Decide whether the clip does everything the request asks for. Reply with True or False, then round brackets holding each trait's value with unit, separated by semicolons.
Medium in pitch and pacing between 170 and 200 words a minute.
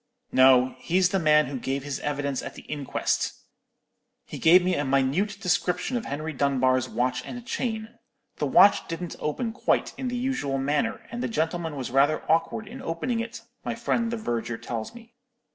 True (165 Hz; 180 wpm)